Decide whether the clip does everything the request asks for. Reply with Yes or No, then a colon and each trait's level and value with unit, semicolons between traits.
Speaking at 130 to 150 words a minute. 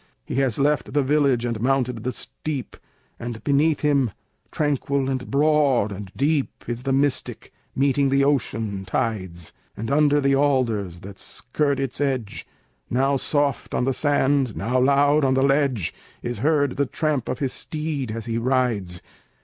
No: average, 160 wpm